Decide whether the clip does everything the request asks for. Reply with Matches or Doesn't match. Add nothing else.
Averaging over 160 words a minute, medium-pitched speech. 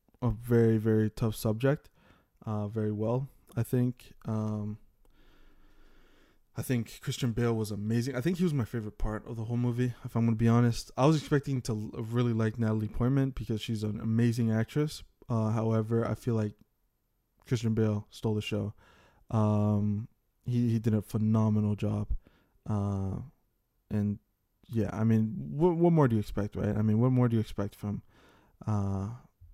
Doesn't match